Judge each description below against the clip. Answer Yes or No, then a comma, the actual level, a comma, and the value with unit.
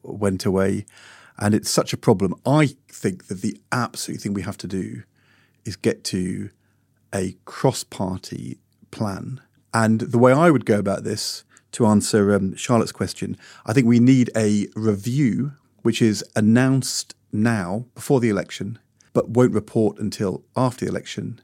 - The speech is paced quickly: No, average, 160 wpm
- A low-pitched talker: Yes, low, 115 Hz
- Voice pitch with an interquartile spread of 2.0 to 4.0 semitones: Yes, average, 3.3 semitones